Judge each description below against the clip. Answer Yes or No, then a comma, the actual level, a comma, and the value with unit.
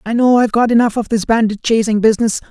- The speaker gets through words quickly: Yes, fast, 240 wpm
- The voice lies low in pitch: No, high, 225 Hz